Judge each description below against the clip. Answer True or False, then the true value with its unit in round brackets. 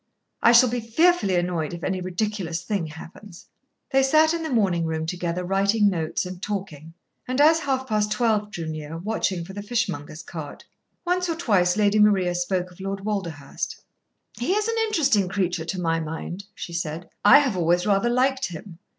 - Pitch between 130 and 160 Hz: False (195 Hz)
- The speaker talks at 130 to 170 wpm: False (185 wpm)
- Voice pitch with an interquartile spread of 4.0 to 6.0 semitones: True (5.1 semitones)